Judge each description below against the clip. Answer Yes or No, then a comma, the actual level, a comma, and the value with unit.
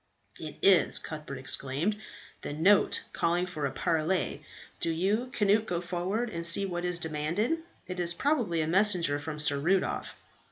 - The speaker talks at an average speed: Yes, average, 160 wpm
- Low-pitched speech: No, medium, 175 Hz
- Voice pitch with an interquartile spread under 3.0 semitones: No, average, 4.0 semitones